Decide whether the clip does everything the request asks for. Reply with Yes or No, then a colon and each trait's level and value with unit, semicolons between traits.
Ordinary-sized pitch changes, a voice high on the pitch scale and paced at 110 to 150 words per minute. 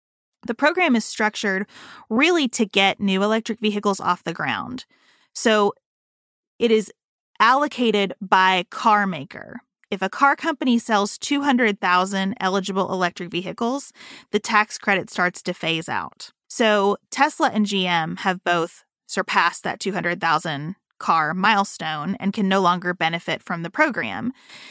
Yes: average, 4.4 semitones; high, 200 Hz; slow, 135 wpm